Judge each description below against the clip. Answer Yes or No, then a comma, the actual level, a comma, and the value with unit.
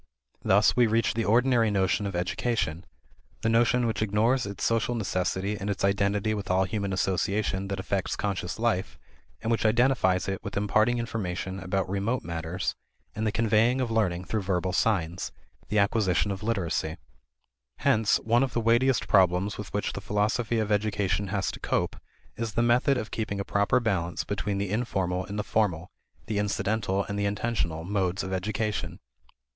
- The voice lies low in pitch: Yes, low, 100 Hz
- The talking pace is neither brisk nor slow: Yes, average, 175 wpm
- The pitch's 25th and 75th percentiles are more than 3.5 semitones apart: No, average, 2.9 semitones